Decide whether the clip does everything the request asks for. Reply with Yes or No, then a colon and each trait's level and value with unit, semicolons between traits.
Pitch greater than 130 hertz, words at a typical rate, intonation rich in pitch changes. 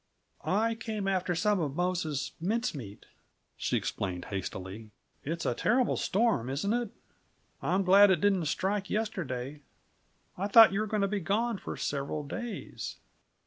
Yes: high, 190 Hz; average, 150 wpm; wide, 6.6 semitones